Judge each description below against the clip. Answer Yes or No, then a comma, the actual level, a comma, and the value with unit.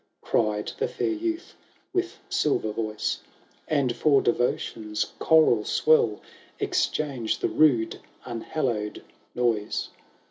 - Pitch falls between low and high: No, low, 120 Hz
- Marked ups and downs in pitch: Yes, wide, 6.3 semitones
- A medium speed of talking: No, slow, 105 wpm